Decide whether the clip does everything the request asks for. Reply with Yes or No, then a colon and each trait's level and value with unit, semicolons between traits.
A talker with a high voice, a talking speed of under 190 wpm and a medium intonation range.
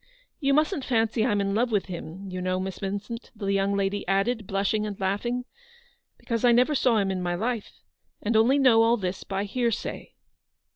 No: high, 210 Hz; average, 200 wpm; average, 3.6 semitones